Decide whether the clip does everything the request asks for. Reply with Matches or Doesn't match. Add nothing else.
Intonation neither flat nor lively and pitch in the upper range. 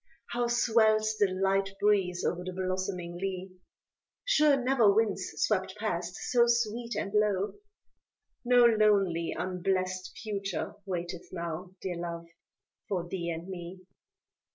Matches